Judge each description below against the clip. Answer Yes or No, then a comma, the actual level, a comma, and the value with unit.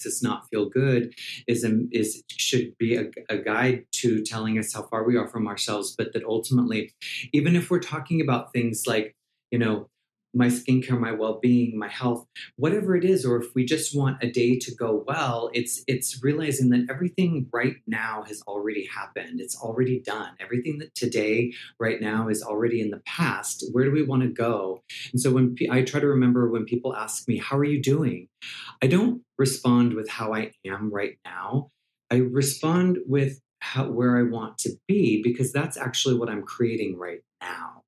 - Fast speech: No, average, 195 wpm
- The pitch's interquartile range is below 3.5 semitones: Yes, average, 3.1 semitones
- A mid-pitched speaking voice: No, low, 125 Hz